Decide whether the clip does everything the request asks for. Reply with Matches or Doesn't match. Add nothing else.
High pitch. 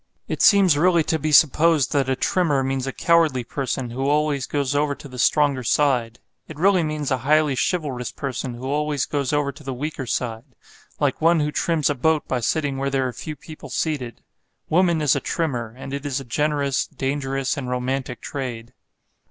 Doesn't match